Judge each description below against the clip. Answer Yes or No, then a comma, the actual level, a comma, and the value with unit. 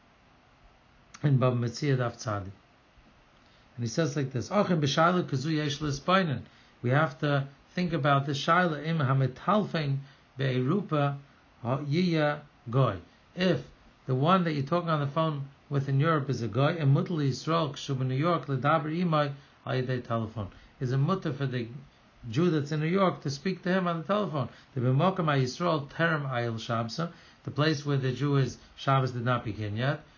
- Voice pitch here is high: No, medium, 140 Hz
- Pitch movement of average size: Yes, average, 4.0 semitones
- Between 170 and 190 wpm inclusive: Yes, average, 180 wpm